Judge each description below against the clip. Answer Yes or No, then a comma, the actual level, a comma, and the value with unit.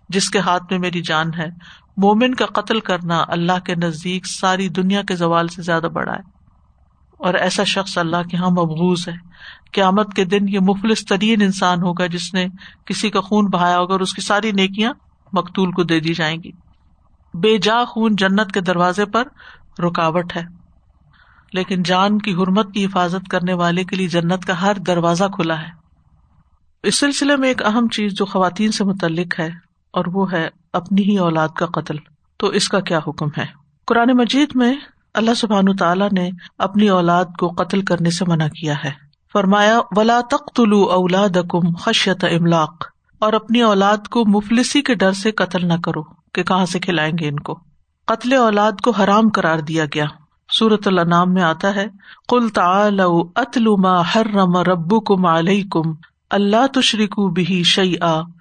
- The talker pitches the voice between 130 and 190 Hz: Yes, medium, 185 Hz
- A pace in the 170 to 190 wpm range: Yes, average, 175 wpm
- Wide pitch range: No, average, 3.3 semitones